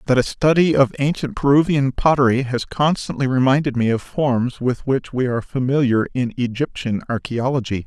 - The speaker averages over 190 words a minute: No, average, 160 wpm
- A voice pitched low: Yes, low, 130 Hz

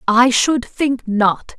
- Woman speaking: Yes, female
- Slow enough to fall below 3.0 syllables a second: Yes, 2.8 syllables/s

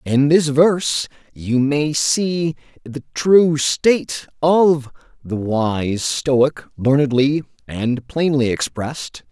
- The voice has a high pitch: No, medium, 140 Hz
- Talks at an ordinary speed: No, slow, 110 wpm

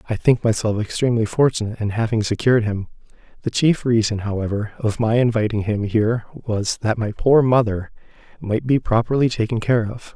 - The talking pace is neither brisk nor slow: Yes, average, 170 wpm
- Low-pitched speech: Yes, low, 115 Hz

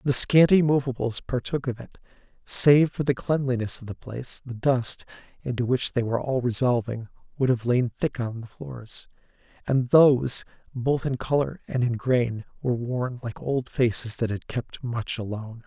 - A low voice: Yes, low, 125 Hz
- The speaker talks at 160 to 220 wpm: Yes, average, 170 wpm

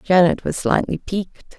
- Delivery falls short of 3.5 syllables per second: No, 5.1 syllables/s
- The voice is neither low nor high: Yes, medium, 180 Hz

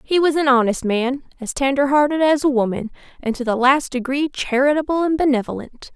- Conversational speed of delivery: Yes, average, 190 wpm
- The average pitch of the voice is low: No, very high, 270 Hz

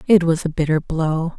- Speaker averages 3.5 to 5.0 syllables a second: Yes, 4.9 syllables/s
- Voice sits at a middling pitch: Yes, medium, 165 Hz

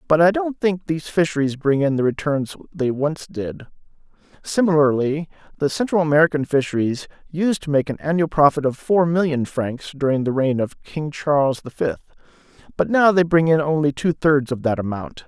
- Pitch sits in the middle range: Yes, medium, 150 Hz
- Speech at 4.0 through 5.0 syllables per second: No, 5.2 syllables/s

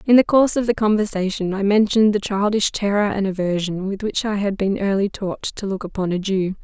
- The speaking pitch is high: Yes, high, 200 Hz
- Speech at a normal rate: No, fast, 225 wpm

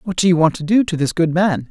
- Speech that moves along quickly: Yes, fast, 355 wpm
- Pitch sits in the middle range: Yes, medium, 175 Hz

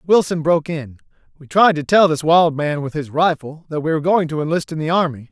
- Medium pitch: Yes, medium, 160 Hz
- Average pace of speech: No, fast, 250 wpm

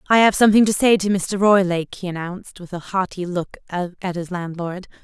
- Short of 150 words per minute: No, fast, 205 wpm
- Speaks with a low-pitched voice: No, medium, 185 Hz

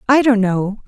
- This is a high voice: Yes, high, 225 Hz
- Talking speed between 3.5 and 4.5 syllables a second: Yes, 4.4 syllables/s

